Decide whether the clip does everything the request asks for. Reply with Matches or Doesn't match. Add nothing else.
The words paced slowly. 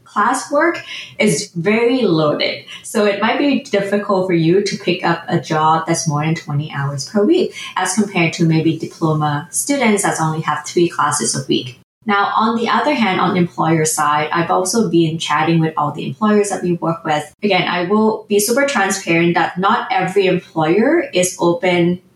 Doesn't match